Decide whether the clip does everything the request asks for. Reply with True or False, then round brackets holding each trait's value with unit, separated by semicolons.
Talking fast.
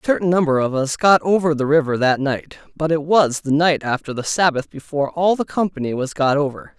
True (230 wpm)